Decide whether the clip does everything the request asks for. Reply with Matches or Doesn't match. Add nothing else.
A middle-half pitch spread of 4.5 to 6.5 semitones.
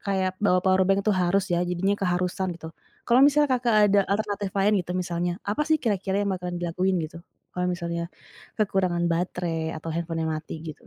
Doesn't match